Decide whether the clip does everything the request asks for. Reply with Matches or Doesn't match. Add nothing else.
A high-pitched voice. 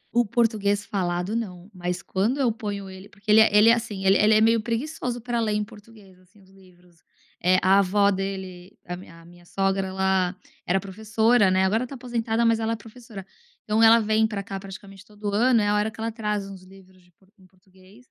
Matches